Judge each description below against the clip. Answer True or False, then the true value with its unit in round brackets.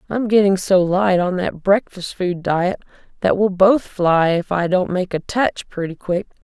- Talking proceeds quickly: False (195 wpm)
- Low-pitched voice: False (185 Hz)